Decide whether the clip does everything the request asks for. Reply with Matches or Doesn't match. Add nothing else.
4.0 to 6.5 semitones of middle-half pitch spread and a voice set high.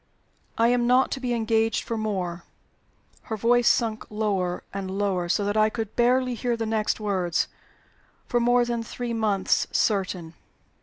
Doesn't match